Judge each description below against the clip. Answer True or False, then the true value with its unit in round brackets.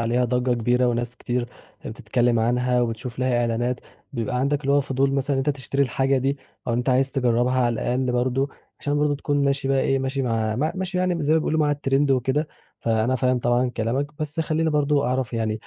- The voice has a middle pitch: False (130 Hz)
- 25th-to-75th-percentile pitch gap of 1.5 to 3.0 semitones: True (2.6 semitones)